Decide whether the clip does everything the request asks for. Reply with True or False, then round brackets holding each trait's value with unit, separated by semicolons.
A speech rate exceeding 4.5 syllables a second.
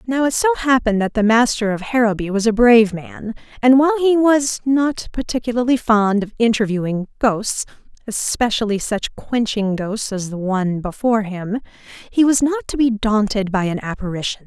True (5.2 syllables/s)